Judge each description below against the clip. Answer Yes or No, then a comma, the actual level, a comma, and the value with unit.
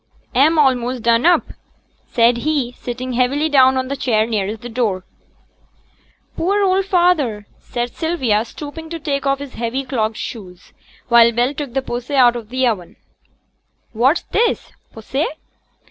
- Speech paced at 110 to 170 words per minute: Yes, average, 150 wpm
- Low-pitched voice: No, very high, 255 Hz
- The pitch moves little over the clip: No, average, 3.7 semitones